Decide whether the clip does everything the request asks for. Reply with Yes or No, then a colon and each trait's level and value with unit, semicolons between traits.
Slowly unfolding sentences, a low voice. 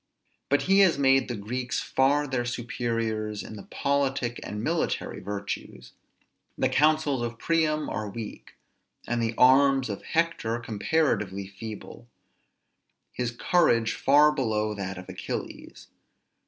Yes: slow, 125 wpm; low, 120 Hz